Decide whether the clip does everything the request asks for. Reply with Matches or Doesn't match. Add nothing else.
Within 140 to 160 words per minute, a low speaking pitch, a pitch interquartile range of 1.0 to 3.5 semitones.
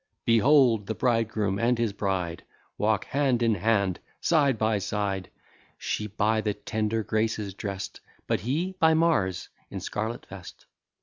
Matches